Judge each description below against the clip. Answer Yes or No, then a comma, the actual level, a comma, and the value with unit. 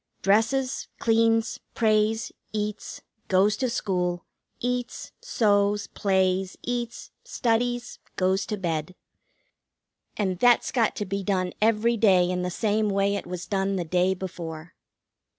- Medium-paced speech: No, slow, 130 wpm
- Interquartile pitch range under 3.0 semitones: No, average, 3.6 semitones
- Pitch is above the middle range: Yes, high, 205 Hz